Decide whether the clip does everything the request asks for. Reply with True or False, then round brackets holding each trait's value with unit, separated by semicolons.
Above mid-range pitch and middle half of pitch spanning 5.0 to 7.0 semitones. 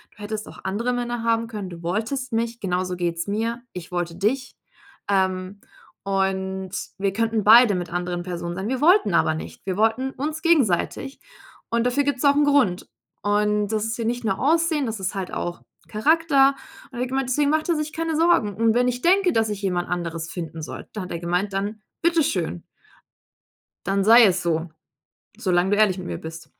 True (210 Hz; 5.4 semitones)